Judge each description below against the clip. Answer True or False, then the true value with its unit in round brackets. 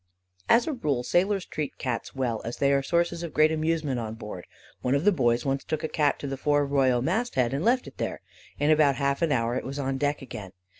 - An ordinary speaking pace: False (245 wpm)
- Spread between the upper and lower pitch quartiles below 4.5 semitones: True (3.6 semitones)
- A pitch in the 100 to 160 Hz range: True (140 Hz)